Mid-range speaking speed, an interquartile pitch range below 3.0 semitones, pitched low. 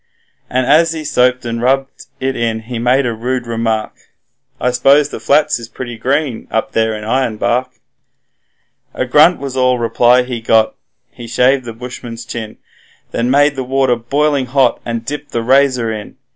Yes: average, 170 wpm; narrow, 2.6 semitones; low, 125 Hz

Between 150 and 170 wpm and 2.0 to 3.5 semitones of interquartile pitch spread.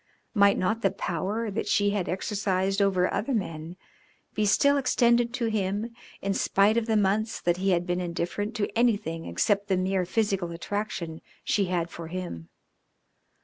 Yes: average, 165 wpm; average, 3.1 semitones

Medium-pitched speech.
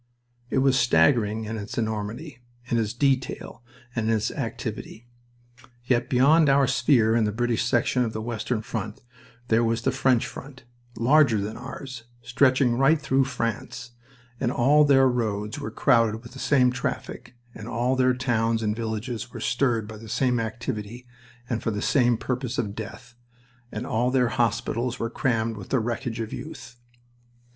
No: low, 120 Hz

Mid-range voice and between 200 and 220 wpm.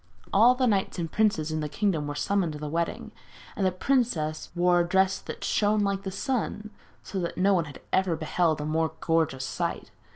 Yes: medium, 180 Hz; fast, 205 wpm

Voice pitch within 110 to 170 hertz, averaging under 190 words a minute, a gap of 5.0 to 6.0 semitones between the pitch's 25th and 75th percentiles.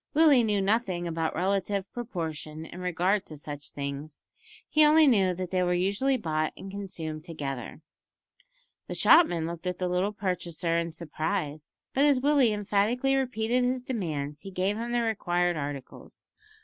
No: medium, 185 Hz; average, 160 wpm; wide, 5.6 semitones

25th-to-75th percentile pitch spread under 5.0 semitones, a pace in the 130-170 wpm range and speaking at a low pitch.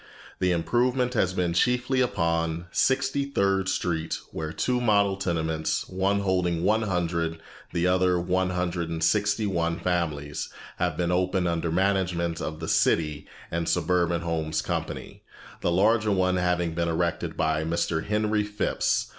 Yes: average, 3.0 semitones; average, 150 wpm; very low, 90 Hz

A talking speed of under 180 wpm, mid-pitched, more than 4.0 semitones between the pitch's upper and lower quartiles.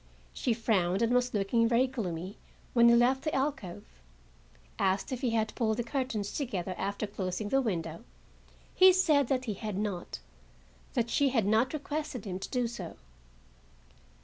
No: average, 165 wpm; high, 230 Hz; average, 4.4 semitones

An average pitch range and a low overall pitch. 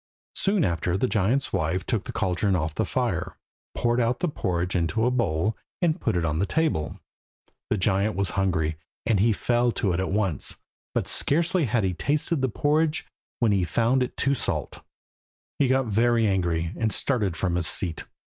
No: wide, 5.8 semitones; low, 105 Hz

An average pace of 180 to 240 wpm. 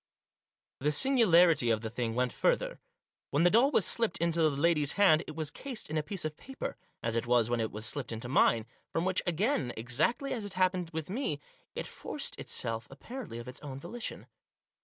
Yes: average, 200 wpm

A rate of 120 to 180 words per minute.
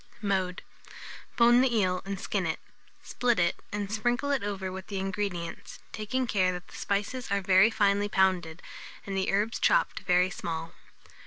Yes: average, 165 wpm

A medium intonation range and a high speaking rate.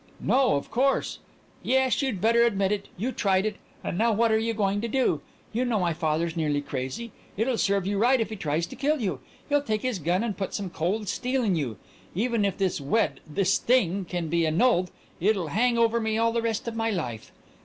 Yes: average, 4.9 semitones; fast, 230 wpm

